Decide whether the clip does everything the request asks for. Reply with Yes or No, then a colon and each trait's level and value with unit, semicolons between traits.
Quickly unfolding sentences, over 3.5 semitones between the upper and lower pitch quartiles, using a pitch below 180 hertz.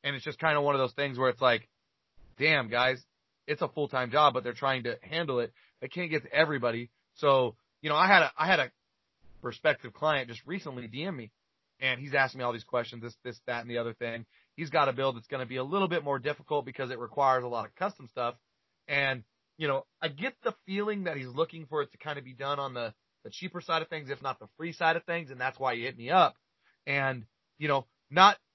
Yes: fast, 255 wpm; average, 4.1 semitones; low, 135 Hz